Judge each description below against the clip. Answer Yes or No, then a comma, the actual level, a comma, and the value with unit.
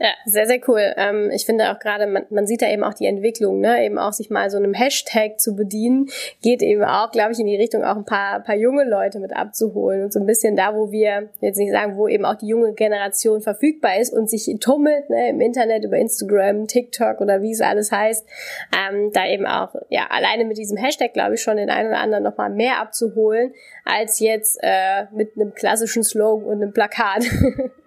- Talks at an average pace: No, fast, 225 wpm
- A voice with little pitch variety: Yes, narrow, 1.6 semitones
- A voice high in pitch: Yes, high, 215 Hz